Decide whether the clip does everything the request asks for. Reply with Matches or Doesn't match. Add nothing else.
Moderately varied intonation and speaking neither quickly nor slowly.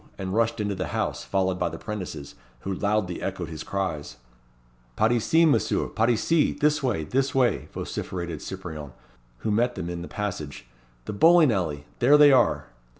Doesn't match